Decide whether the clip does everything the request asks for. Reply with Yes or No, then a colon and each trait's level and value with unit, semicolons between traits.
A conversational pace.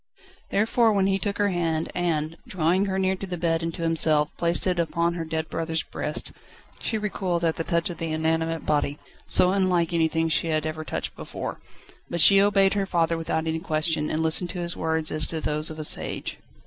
No: fast, 210 wpm